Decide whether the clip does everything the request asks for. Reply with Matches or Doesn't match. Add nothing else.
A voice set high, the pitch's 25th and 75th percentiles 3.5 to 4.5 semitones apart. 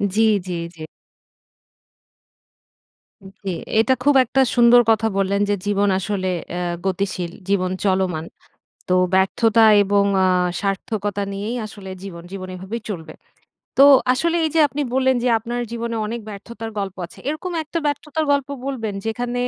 Matches